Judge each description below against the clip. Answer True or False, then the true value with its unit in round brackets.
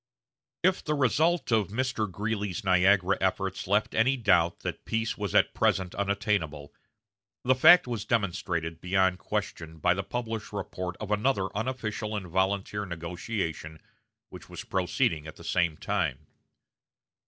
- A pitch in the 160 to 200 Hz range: False (100 Hz)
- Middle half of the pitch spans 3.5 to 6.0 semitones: True (3.8 semitones)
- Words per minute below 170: True (140 wpm)